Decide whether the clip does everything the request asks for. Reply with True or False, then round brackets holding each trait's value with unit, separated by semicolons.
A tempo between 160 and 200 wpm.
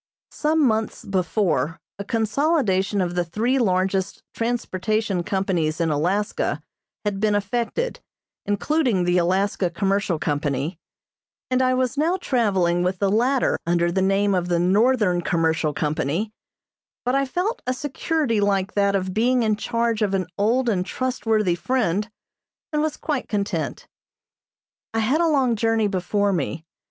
False (145 wpm)